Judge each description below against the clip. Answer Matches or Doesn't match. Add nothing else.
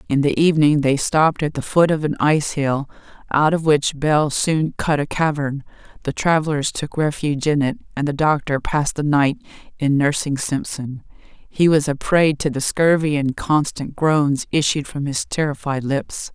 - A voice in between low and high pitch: Matches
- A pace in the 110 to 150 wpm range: Doesn't match